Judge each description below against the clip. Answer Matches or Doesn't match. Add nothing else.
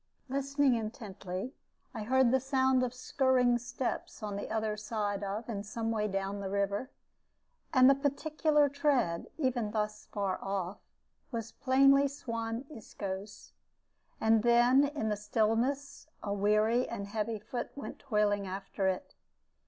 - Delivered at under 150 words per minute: Matches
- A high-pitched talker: Matches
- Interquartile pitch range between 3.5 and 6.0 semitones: Matches